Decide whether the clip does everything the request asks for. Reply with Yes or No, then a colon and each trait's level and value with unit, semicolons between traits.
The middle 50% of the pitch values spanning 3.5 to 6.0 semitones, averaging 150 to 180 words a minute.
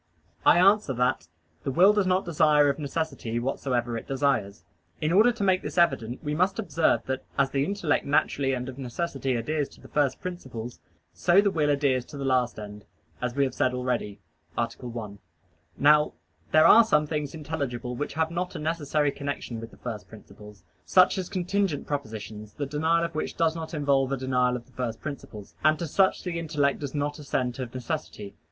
No: average, 4.5 semitones; average, 195 wpm